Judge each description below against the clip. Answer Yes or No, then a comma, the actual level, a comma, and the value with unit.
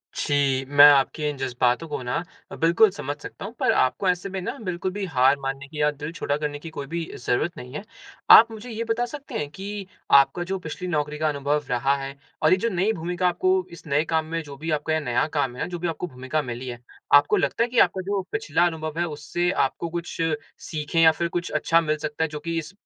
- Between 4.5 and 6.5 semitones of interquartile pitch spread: No, average, 3.8 semitones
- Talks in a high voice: No, medium, 160 Hz